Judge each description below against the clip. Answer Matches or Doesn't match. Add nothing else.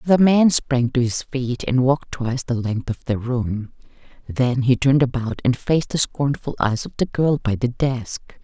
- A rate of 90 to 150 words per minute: Doesn't match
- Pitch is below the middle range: Matches